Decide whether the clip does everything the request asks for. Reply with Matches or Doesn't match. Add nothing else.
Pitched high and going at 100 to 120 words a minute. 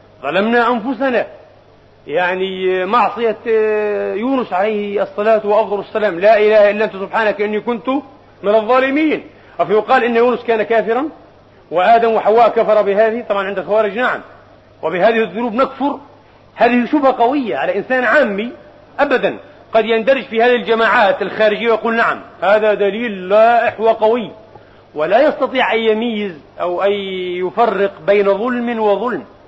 Doesn't match